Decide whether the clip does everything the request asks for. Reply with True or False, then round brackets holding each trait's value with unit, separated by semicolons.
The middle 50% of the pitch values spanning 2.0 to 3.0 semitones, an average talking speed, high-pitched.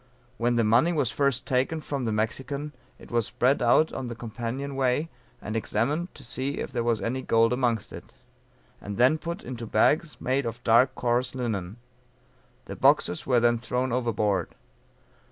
False (2.7 semitones; 170 wpm; 125 Hz)